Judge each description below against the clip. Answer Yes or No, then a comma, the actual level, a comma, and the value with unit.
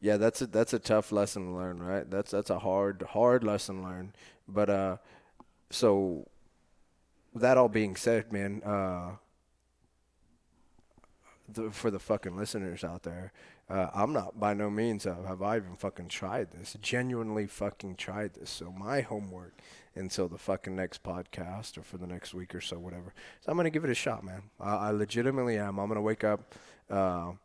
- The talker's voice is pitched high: No, low, 100 Hz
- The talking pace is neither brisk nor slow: Yes, average, 190 wpm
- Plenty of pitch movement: No, average, 2.8 semitones